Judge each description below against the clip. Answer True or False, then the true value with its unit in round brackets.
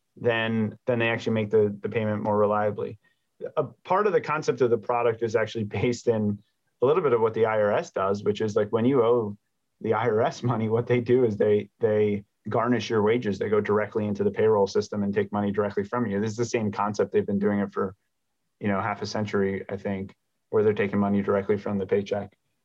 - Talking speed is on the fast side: True (230 wpm)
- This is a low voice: True (110 Hz)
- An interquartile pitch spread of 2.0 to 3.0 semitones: True (2.7 semitones)